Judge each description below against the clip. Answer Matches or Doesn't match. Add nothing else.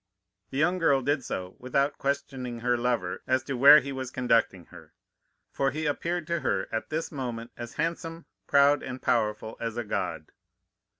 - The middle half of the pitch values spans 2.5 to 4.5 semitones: Matches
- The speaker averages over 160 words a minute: Matches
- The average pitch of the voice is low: Matches